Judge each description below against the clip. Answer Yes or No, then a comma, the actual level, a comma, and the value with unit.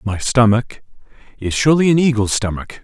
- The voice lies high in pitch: No, low, 120 Hz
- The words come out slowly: Yes, slow, 125 wpm